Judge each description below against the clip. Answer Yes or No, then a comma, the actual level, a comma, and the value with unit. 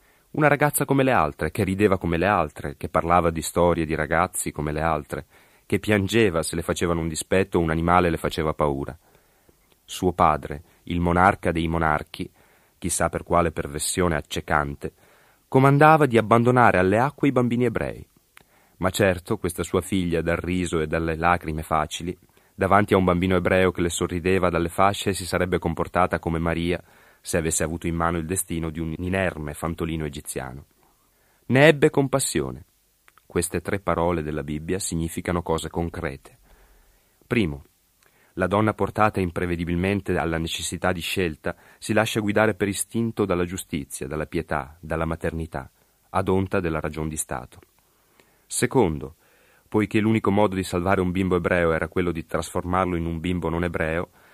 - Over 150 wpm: Yes, average, 160 wpm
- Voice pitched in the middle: No, very low, 90 Hz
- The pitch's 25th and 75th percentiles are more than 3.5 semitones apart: No, average, 2.9 semitones